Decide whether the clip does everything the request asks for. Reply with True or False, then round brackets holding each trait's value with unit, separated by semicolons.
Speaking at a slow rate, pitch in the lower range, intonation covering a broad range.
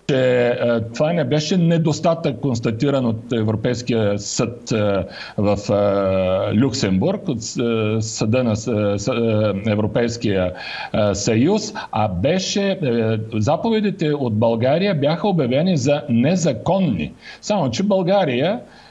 True (90 wpm; 125 Hz; 6.9 semitones)